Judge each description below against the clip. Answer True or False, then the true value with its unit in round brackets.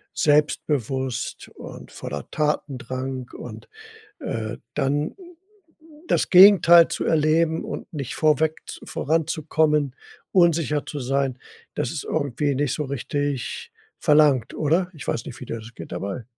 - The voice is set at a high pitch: False (145 Hz)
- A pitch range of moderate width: True (3.2 semitones)